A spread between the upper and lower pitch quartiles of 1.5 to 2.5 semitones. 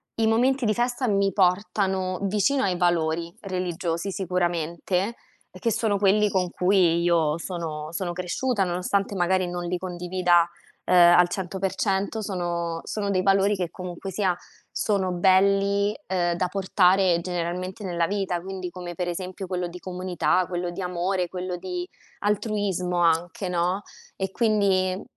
Yes: narrow, 2.1 semitones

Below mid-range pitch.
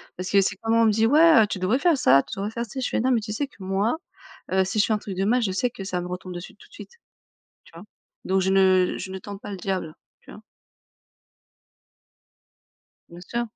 No: high, 200 Hz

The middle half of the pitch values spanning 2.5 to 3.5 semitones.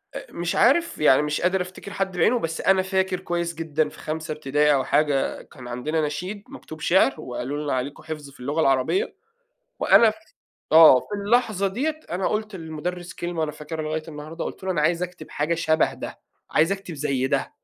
No: average, 4.0 semitones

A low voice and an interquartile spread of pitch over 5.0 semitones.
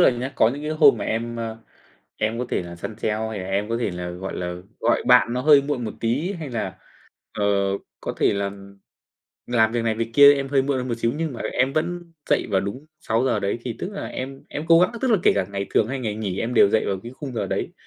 No: low, 120 Hz; average, 4.4 semitones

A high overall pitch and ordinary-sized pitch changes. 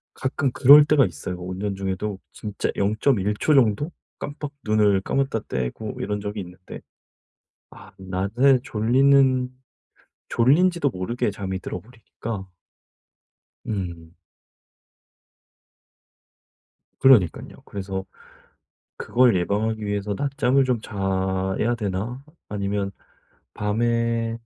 No: low, 105 Hz; average, 4.7 semitones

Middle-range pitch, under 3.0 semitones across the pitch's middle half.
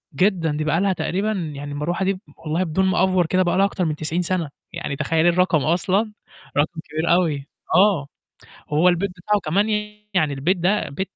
No: medium, 175 Hz; average, 3.3 semitones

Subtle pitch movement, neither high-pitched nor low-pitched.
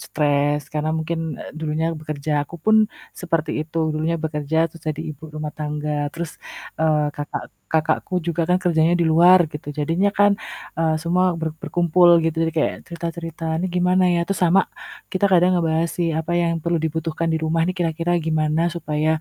Yes: narrow, 1.9 semitones; medium, 165 Hz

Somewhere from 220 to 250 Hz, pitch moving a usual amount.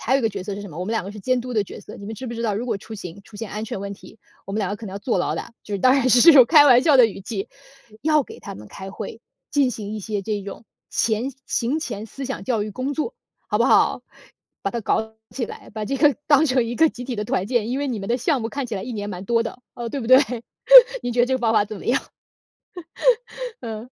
Yes: high, 230 Hz; average, 3.7 semitones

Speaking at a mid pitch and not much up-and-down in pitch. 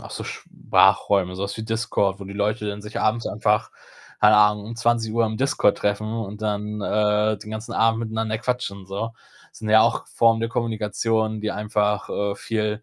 No: low, 110 Hz; narrow, 1.4 semitones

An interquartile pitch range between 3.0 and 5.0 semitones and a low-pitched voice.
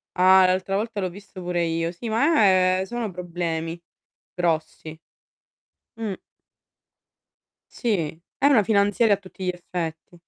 No: average, 3.3 semitones; medium, 185 Hz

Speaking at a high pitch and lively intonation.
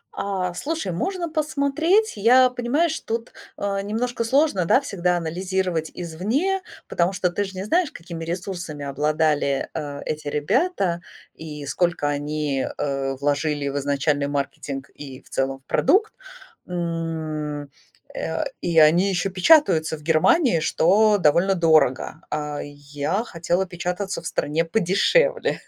No: medium, 175 Hz; wide, 6.0 semitones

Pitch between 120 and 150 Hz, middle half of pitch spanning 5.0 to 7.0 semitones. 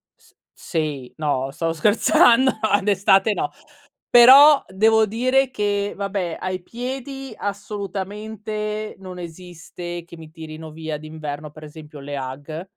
No: high, 190 Hz; wide, 5.5 semitones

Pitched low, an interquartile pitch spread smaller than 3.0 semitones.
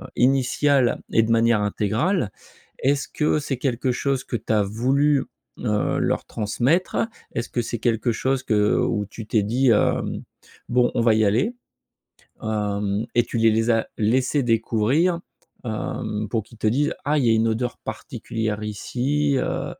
No: low, 115 Hz; average, 3.5 semitones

